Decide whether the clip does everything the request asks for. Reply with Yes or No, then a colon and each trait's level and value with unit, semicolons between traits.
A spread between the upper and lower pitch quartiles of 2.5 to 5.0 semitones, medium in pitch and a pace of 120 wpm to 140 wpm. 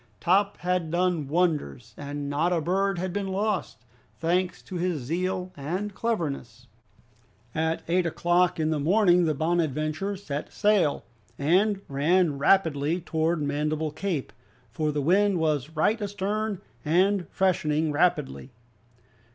Yes: average, 3.9 semitones; medium, 170 Hz; slow, 135 wpm